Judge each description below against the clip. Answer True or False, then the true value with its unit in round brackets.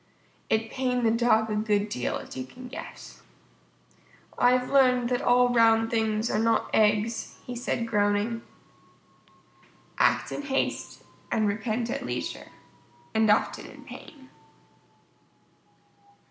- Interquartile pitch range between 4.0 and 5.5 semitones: False (2.4 semitones)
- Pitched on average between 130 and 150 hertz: False (230 Hz)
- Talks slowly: True (125 wpm)